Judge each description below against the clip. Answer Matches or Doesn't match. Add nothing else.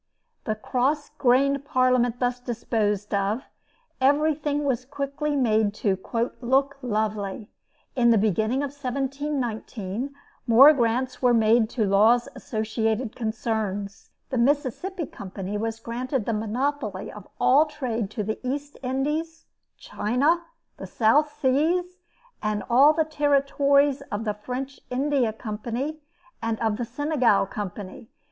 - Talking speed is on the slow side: Matches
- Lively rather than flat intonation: Doesn't match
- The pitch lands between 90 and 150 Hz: Doesn't match